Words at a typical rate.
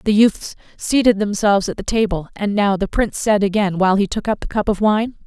No: fast, 240 wpm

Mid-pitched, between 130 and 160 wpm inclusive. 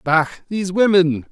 Yes: medium, 175 Hz; slow, 135 wpm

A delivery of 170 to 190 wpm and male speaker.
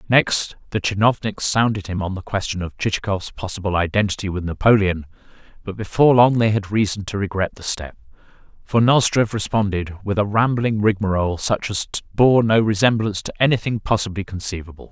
No: average, 160 wpm; male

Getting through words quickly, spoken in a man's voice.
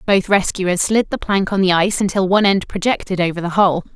No: fast, 230 wpm; female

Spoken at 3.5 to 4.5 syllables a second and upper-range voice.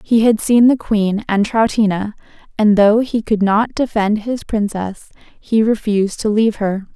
Yes: 4.4 syllables/s; high, 215 Hz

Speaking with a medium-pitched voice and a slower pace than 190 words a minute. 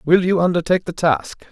No: medium, 165 Hz; average, 200 wpm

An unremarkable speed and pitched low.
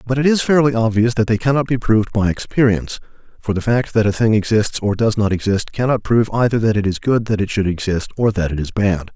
No: fast, 255 wpm; low, 110 Hz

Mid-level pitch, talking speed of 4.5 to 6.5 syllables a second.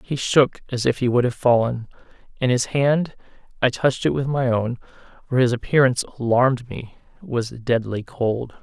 No: low, 125 Hz; 5.0 syllables/s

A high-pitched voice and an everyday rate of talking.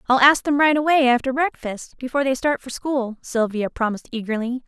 Yes: very high, 260 Hz; average, 195 wpm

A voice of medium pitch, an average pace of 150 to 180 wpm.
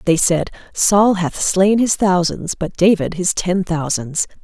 Yes: medium, 180 Hz; average, 160 wpm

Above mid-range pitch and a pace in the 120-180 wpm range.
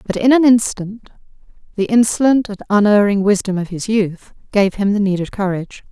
Yes: high, 205 Hz; average, 170 wpm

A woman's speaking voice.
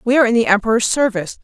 Yes: female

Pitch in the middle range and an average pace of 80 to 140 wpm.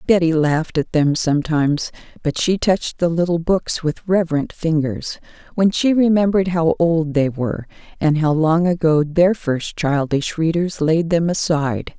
No: medium, 165 Hz; average, 160 wpm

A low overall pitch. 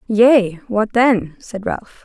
No: high, 220 Hz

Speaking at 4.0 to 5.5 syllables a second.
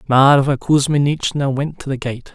Yes: 4.6 syllables/s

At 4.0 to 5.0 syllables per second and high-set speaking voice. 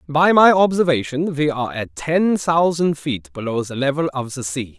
No: 4.8 syllables/s; medium, 145 Hz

